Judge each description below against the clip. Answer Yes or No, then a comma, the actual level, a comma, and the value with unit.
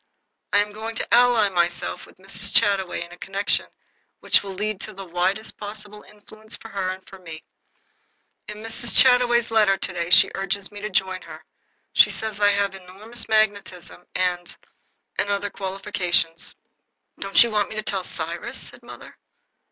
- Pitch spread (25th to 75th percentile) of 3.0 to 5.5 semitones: No, narrow, 2.4 semitones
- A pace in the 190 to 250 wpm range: No, average, 170 wpm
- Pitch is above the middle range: Yes, high, 200 Hz